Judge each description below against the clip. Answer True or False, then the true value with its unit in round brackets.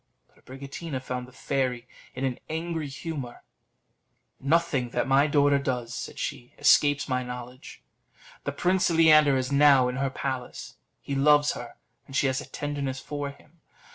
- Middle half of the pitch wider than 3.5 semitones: False (2.4 semitones)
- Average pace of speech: True (160 wpm)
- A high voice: False (140 Hz)